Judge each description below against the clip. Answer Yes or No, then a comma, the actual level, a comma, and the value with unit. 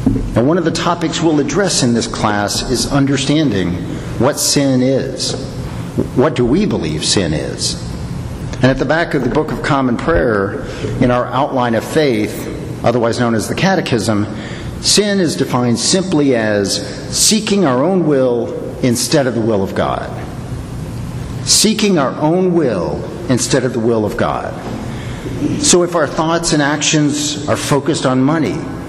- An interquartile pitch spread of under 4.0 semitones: No, average, 4.5 semitones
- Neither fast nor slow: Yes, average, 160 wpm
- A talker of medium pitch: No, low, 130 Hz